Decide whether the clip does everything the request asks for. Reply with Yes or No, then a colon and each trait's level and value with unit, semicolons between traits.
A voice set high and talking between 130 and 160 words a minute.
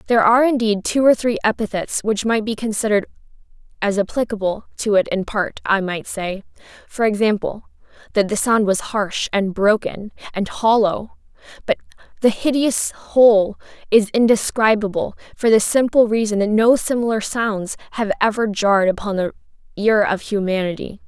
Yes: high, 215 Hz; average, 150 wpm